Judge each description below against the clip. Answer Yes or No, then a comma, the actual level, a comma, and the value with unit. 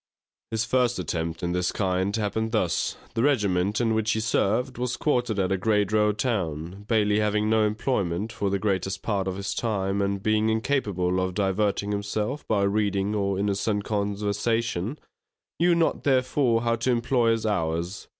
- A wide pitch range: No, average, 2.7 semitones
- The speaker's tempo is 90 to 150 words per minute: No, average, 170 wpm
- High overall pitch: No, low, 105 Hz